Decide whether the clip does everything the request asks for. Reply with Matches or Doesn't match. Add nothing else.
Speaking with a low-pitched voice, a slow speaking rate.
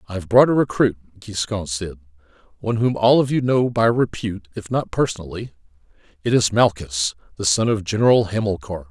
Doesn't match